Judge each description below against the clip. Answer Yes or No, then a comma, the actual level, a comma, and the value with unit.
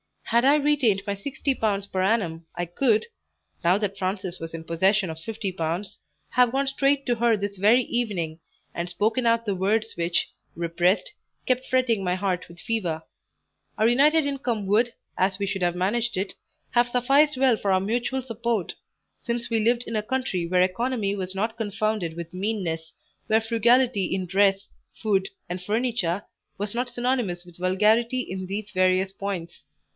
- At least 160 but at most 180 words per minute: Yes, average, 170 wpm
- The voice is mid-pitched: No, high, 205 Hz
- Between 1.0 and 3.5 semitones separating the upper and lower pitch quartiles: No, average, 4.3 semitones